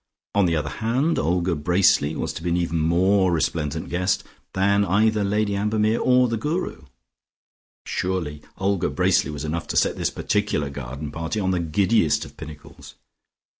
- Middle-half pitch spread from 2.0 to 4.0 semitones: No, average, 4.6 semitones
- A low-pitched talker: Yes, very low, 90 Hz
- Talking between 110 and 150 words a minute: No, average, 165 wpm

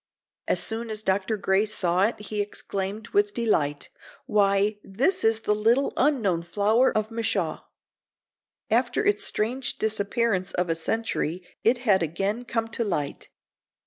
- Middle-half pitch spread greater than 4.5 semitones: No, average, 3.3 semitones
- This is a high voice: Yes, high, 215 Hz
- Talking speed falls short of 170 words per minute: Yes, average, 145 wpm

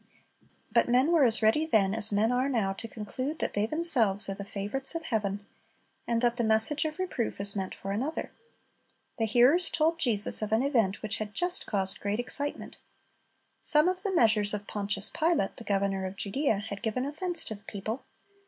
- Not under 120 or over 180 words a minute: No, average, 195 wpm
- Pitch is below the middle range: No, high, 225 Hz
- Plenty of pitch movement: Yes, wide, 5.8 semitones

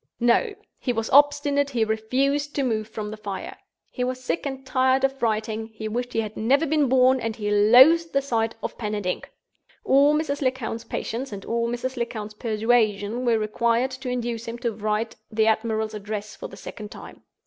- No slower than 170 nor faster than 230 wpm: Yes, average, 195 wpm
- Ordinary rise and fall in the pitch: Yes, average, 3.4 semitones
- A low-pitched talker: No, high, 235 Hz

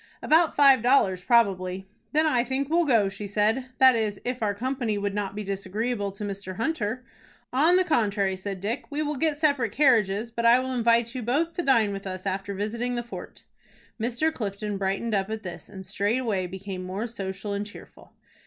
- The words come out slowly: No, average, 195 wpm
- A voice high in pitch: Yes, high, 220 Hz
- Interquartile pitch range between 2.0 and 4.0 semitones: No, average, 4.4 semitones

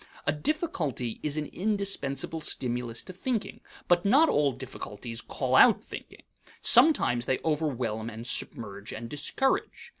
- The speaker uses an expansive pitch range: Yes, wide, 8.1 semitones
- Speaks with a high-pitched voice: No, medium, 140 Hz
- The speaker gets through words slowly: Yes, slow, 130 wpm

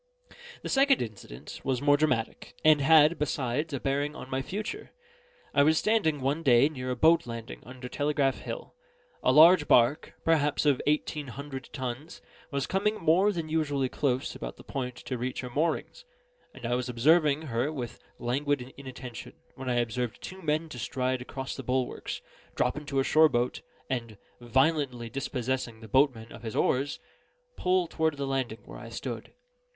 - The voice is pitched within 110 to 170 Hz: Yes, low, 135 Hz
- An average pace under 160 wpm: No, average, 170 wpm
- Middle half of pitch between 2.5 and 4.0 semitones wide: Yes, average, 3.6 semitones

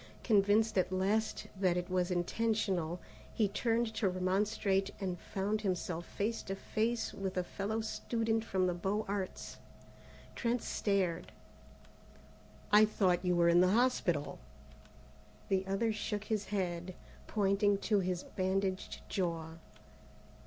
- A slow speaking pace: Yes, slow, 130 wpm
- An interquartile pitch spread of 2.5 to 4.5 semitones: Yes, average, 2.9 semitones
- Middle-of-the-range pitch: No, high, 195 Hz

